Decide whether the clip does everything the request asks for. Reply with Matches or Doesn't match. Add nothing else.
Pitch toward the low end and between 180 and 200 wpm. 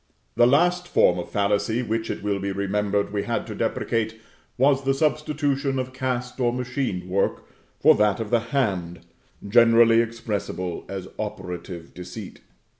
Doesn't match